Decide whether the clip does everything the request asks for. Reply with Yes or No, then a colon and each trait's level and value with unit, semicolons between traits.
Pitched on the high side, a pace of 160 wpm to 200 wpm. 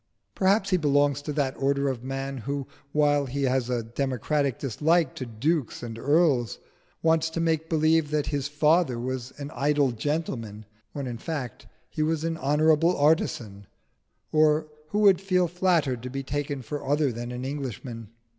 No: medium, 145 Hz; average, 165 wpm